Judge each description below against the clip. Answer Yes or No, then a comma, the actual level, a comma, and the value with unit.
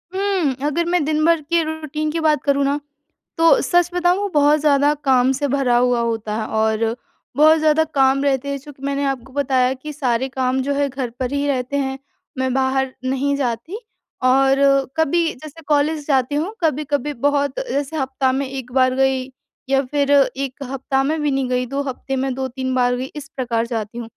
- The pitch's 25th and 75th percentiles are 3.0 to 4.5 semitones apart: No, narrow, 2.4 semitones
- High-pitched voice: Yes, very high, 275 Hz